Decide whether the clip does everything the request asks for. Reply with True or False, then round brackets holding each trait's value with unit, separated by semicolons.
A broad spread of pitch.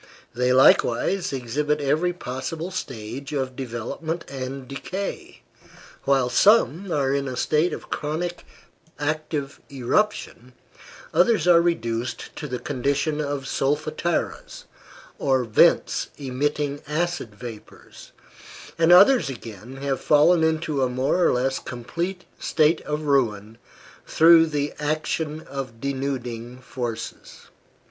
False (3.9 semitones)